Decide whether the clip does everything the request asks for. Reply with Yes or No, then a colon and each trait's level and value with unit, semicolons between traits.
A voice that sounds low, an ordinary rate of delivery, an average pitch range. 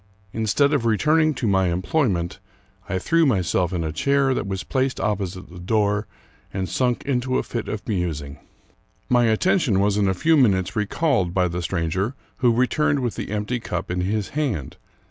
No: low, 105 Hz; average, 180 wpm; wide, 5.8 semitones